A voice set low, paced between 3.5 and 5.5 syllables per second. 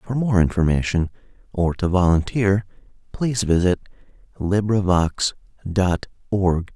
Yes: very low, 95 Hz; 4.4 syllables/s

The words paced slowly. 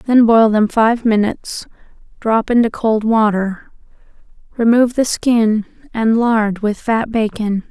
Yes: slow, 130 wpm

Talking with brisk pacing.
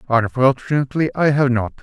No: slow, 130 wpm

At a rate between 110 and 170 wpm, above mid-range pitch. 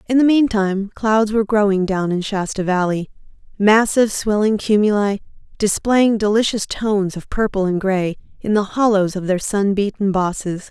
Yes: average, 155 wpm; high, 205 Hz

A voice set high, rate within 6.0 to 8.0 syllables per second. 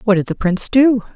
Yes: high, 220 Hz; 6.3 syllables/s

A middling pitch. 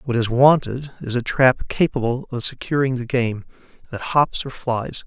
No: low, 125 Hz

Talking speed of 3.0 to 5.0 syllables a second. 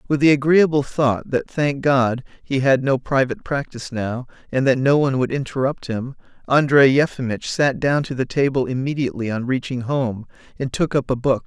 No: 5.3 syllables/s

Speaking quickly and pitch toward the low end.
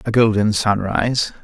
No: slow, 125 wpm; low, 105 Hz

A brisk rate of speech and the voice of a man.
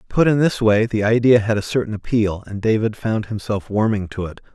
Yes: fast, 225 wpm; male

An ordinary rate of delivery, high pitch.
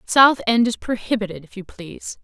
Yes: average, 190 wpm; high, 215 Hz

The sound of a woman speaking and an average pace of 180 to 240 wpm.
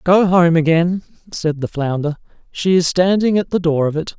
No: male; average, 200 wpm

